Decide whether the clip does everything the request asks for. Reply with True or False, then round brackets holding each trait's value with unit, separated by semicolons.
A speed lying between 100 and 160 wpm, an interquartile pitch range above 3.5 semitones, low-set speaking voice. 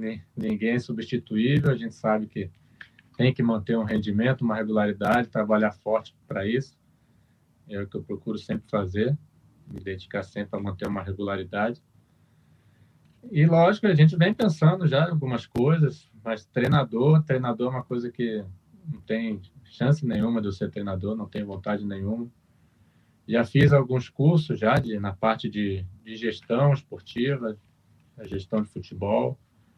True (155 wpm; 3.9 semitones; 115 Hz)